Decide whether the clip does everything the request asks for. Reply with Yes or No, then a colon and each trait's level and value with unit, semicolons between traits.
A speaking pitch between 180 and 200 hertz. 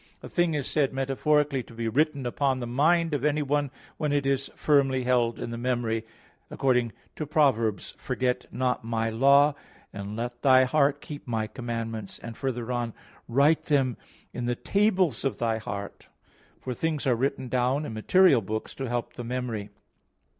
No: low, 130 Hz